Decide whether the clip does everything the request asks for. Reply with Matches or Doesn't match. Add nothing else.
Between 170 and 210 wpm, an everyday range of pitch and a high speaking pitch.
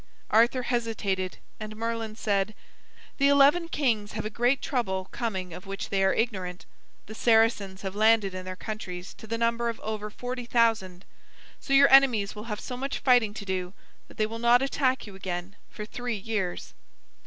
Matches